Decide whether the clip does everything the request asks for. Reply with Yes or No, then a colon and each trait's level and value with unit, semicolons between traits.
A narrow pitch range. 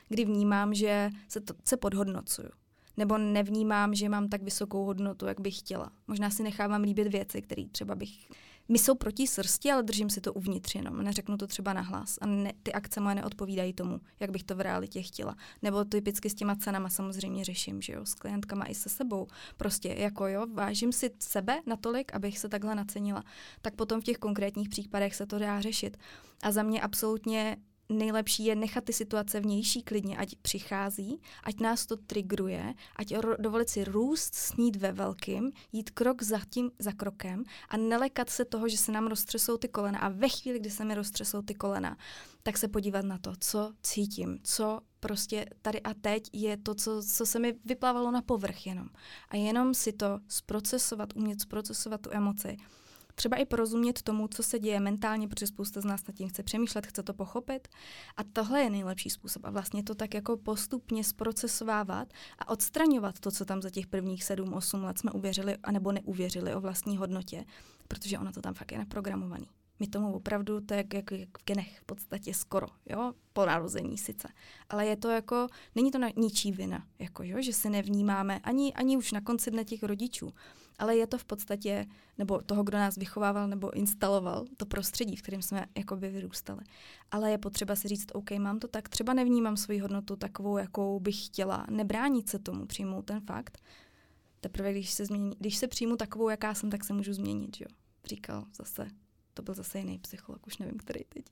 Yes: narrow, 2.0 semitones